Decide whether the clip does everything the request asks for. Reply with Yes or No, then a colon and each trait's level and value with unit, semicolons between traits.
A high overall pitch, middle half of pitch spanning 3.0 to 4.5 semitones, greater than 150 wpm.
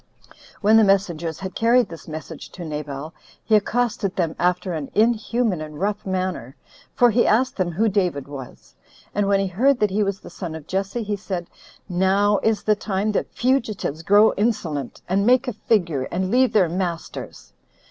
Yes: high, 195 Hz; average, 4.0 semitones; average, 180 wpm